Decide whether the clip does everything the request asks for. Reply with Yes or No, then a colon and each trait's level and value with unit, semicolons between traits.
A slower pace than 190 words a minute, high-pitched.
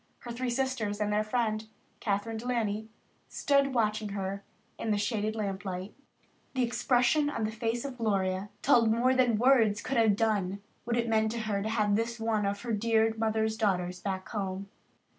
No: average, 195 wpm; high, 220 Hz